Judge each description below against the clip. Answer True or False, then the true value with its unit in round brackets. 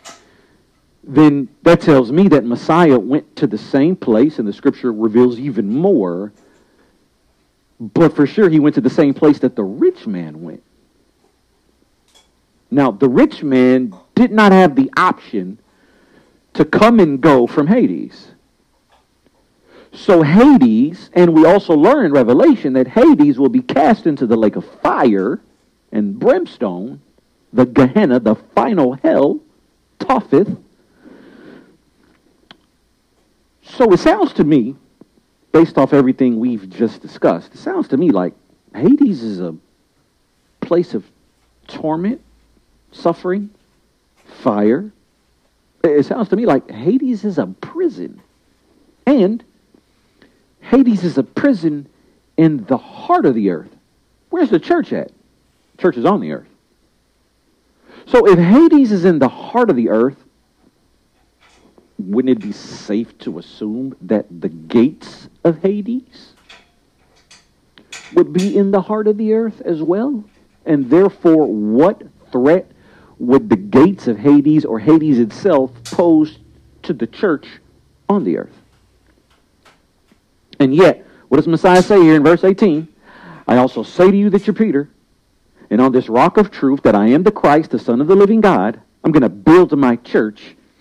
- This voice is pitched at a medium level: True (165 Hz)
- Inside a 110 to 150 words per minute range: True (145 wpm)